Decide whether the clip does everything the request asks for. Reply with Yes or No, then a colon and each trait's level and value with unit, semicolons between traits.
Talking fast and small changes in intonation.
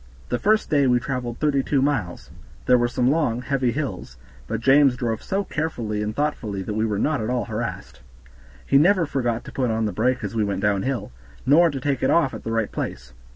No: fast, 220 wpm; average, 4.3 semitones